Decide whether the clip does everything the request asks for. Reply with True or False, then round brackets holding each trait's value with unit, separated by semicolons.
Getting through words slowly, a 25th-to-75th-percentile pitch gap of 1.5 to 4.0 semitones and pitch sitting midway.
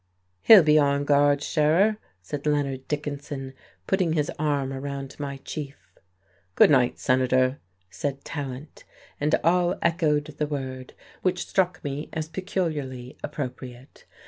True (125 wpm; 2.4 semitones; 145 Hz)